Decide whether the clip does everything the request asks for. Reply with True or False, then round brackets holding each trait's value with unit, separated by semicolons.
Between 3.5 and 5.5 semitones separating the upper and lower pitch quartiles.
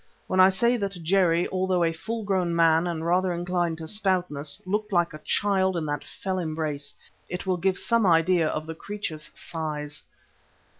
False (2.8 semitones)